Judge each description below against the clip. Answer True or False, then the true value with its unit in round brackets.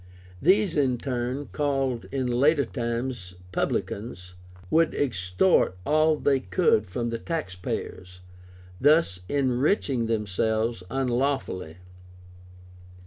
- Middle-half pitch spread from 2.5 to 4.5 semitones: False (5.0 semitones)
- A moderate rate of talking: False (95 wpm)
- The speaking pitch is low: True (125 Hz)